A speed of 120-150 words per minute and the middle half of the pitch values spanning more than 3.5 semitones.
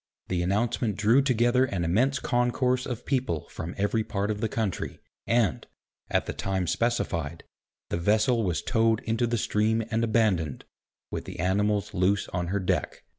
No: average, 165 wpm; average, 4.1 semitones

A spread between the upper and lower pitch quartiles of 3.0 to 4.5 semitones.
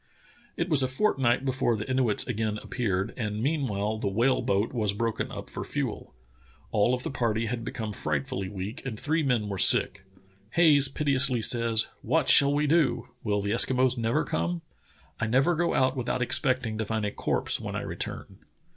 Yes: average, 3.8 semitones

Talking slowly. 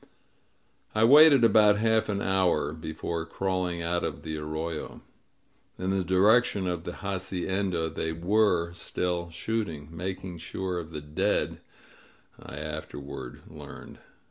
Yes: slow, 125 wpm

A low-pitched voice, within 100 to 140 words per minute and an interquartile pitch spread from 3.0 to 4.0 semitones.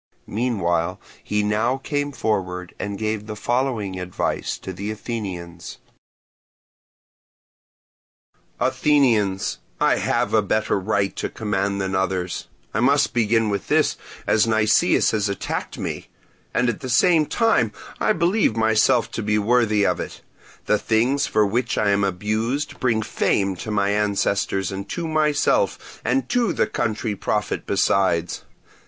Yes: low, 105 Hz; slow, 135 wpm; average, 3.5 semitones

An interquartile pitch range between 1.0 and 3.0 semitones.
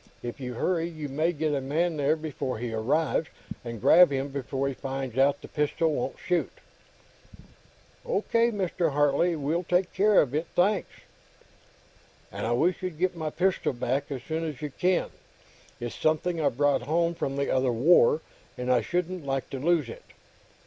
No: average, 4.2 semitones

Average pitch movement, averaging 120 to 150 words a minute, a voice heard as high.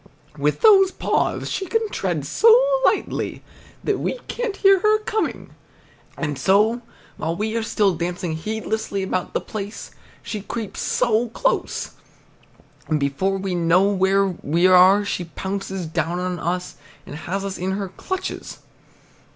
Yes: average, 3.8 semitones; average, 145 wpm; high, 195 Hz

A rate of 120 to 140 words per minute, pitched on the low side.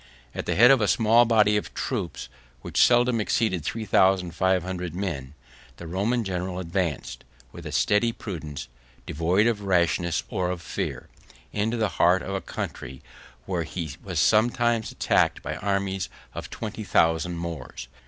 No: average, 160 wpm; very low, 95 Hz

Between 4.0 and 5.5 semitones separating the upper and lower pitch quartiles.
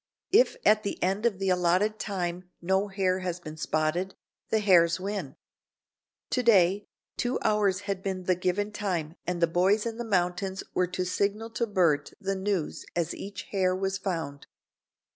No: narrow, 2.5 semitones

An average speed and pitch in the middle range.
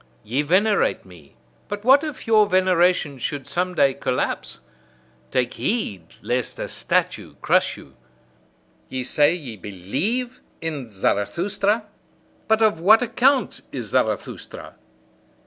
No: slow, 120 wpm; medium, 170 Hz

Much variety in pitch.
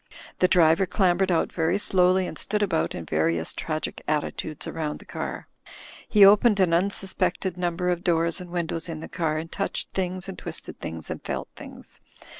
No: average, 2.8 semitones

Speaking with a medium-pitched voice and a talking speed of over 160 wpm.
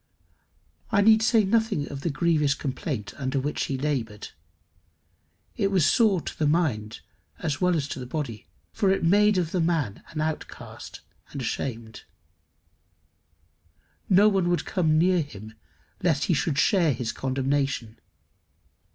No: medium, 155 Hz; average, 145 wpm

